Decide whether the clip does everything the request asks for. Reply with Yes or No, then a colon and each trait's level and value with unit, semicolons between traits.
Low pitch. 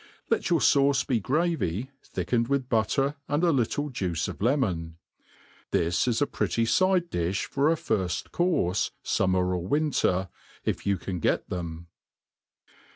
Yes: low, 115 Hz